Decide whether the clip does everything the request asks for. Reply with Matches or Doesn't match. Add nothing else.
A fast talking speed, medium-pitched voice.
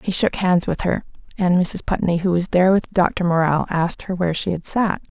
Matches